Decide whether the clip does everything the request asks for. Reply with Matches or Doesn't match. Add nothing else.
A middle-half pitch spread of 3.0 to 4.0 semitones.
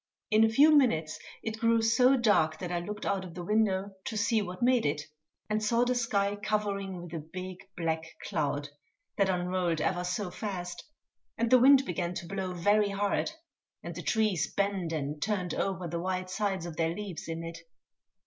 Matches